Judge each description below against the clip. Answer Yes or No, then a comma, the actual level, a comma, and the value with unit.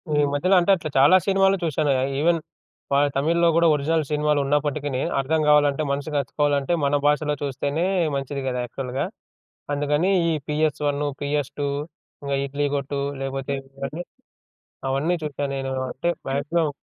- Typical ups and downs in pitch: No, narrow, 2.0 semitones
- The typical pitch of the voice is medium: Yes, medium, 145 Hz